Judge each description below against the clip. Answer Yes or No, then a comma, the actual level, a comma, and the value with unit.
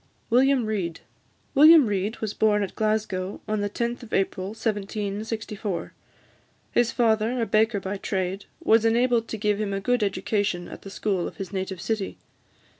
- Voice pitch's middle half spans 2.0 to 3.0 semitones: Yes, narrow, 2.4 semitones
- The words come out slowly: No, average, 165 wpm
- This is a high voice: Yes, high, 215 Hz